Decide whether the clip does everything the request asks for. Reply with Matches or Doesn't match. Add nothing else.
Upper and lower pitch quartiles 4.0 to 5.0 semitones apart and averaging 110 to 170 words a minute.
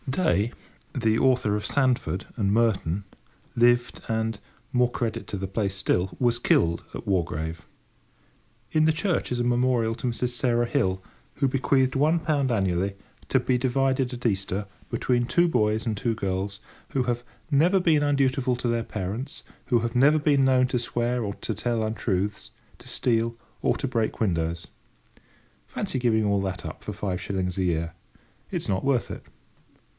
Matches